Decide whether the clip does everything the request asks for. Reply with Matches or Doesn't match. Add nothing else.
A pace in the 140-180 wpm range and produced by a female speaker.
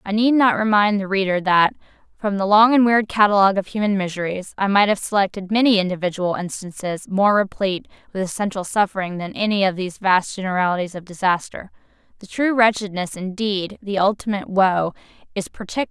Matches